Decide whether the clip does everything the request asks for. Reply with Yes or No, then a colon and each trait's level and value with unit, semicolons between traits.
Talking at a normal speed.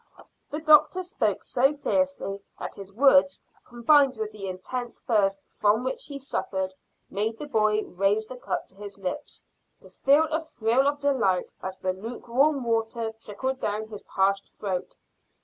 Yes: average, 160 wpm